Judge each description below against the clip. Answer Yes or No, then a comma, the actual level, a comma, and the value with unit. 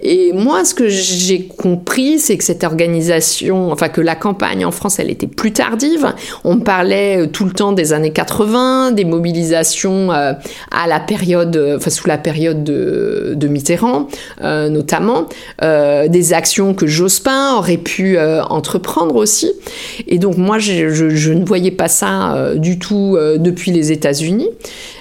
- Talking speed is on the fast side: No, average, 165 wpm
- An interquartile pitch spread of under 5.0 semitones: Yes, average, 4.6 semitones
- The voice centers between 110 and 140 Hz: No, medium, 180 Hz